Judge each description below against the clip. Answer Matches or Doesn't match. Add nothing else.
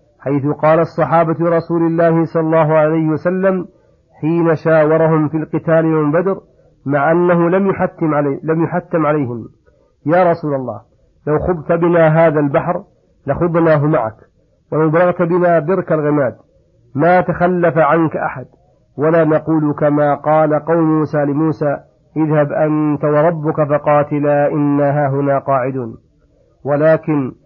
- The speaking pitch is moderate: Matches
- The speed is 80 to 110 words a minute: Doesn't match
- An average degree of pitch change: Doesn't match